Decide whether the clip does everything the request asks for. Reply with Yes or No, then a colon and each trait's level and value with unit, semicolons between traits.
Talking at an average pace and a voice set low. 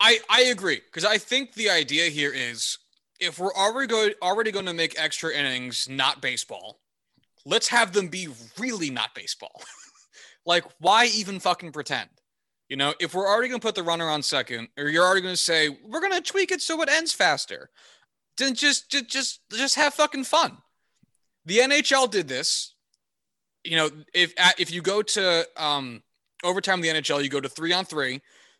No: average, 190 wpm; medium, 185 Hz